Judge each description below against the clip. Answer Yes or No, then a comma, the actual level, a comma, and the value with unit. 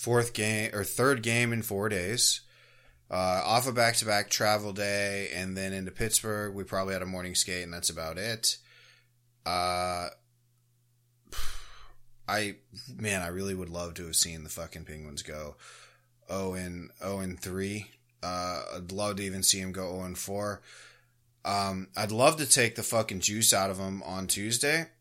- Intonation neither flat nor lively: Yes, average, 4.1 semitones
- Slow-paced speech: No, average, 165 wpm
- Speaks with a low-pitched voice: Yes, low, 100 Hz